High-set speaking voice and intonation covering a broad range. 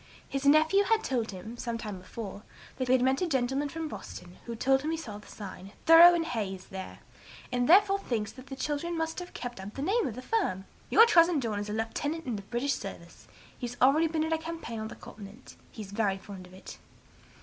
Yes: very high, 255 Hz; wide, 7.2 semitones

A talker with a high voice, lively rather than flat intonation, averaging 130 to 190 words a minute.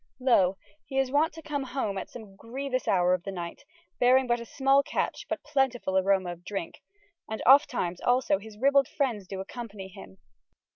Yes: high, 235 Hz; wide, 5.8 semitones; average, 185 wpm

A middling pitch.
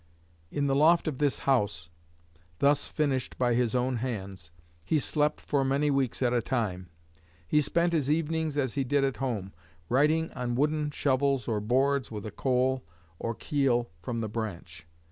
No: low, 130 Hz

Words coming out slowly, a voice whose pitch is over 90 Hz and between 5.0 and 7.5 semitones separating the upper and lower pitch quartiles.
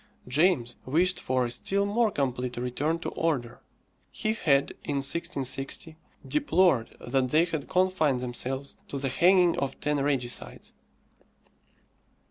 Yes: slow, 125 wpm; medium, 140 Hz; wide, 5.4 semitones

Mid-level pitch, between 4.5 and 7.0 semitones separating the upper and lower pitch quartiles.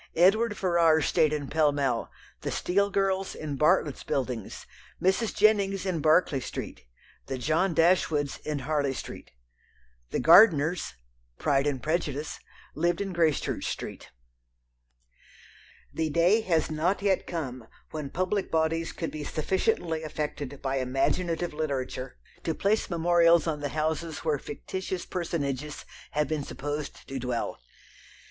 No: medium, 155 Hz; average, 3.5 semitones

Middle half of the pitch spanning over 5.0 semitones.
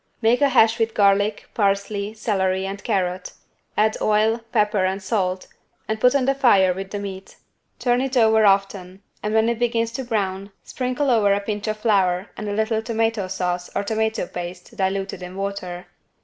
No: average, 2.7 semitones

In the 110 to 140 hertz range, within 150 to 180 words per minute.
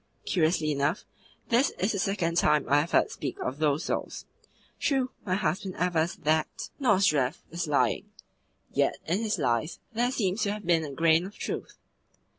No: medium, 170 Hz; average, 170 wpm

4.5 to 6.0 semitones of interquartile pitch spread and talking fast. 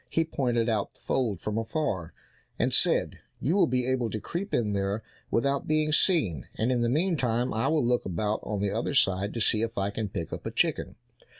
Yes: average, 4.9 semitones; fast, 215 wpm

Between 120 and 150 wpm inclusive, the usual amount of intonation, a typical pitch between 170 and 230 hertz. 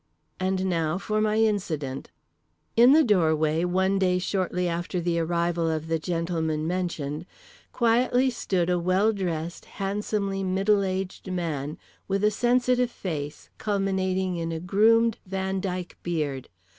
Yes: slow, 135 wpm; average, 3.1 semitones; medium, 185 Hz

